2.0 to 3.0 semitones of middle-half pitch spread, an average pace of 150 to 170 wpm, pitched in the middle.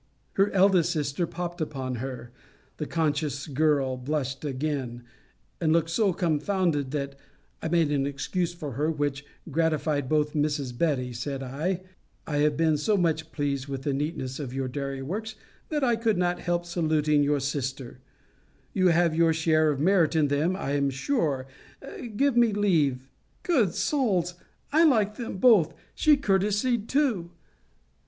No: average, 4.5 semitones; average, 155 wpm; medium, 155 Hz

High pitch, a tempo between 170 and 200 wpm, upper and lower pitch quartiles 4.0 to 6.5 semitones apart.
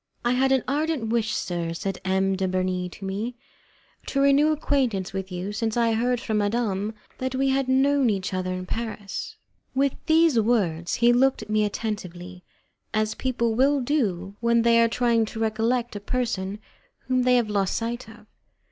Yes: high, 225 Hz; average, 180 wpm; average, 4.5 semitones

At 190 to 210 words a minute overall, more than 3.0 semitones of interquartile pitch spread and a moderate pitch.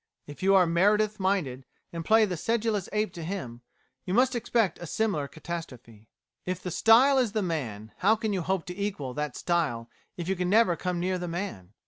Yes: average, 200 wpm; average, 4.8 semitones; medium, 180 Hz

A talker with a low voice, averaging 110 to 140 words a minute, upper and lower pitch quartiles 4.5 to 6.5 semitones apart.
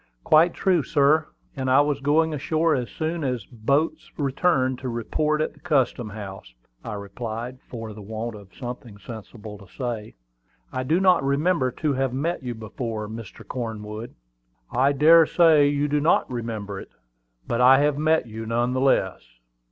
No: low, 130 Hz; average, 175 wpm; average, 4.9 semitones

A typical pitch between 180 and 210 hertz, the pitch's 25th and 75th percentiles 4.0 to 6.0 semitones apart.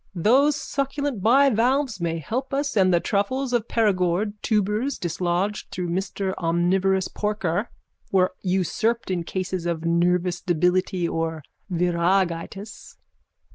Yes: high, 190 Hz; average, 4.4 semitones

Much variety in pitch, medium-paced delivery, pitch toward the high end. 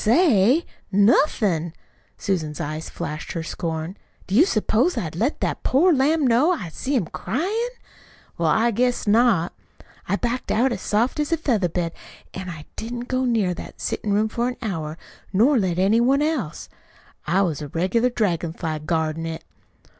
Yes: wide, 6.9 semitones; average, 170 wpm; high, 210 Hz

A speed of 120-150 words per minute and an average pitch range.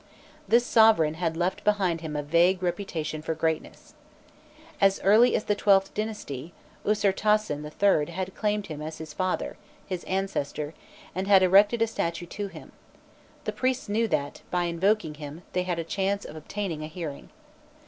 No: average, 165 wpm; average, 4.3 semitones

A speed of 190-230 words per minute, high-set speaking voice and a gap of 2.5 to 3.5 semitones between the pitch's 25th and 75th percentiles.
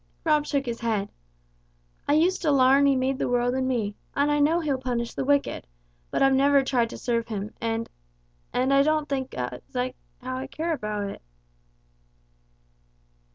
No: average, 175 wpm; very high, 260 Hz; average, 3.2 semitones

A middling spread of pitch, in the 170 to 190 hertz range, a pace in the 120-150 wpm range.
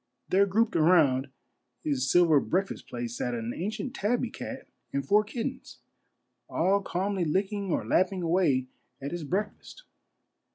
No: wide, 6.1 semitones; medium, 185 Hz; average, 140 wpm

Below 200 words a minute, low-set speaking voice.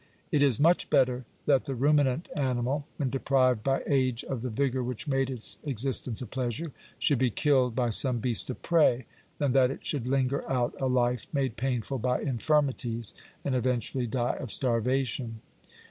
Yes: average, 175 wpm; low, 130 Hz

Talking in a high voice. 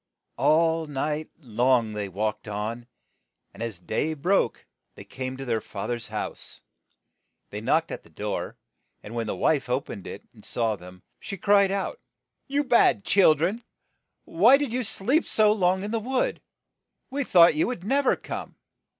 No: medium, 160 Hz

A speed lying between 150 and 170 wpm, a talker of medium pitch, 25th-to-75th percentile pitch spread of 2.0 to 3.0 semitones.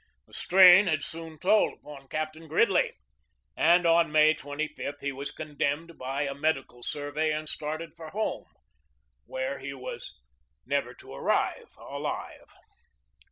No: slow, 135 wpm; medium, 155 Hz; narrow, 2.6 semitones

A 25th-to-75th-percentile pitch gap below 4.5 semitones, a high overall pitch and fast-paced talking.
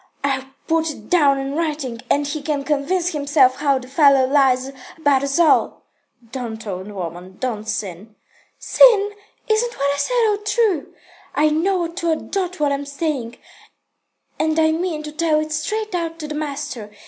No: average, 3.9 semitones; very high, 295 Hz; average, 170 wpm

